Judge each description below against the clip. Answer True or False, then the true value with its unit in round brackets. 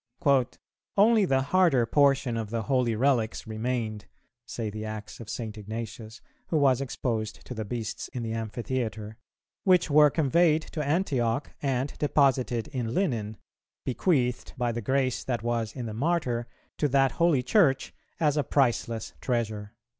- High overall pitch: False (125 Hz)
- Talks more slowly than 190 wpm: True (150 wpm)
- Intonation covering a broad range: False (3.9 semitones)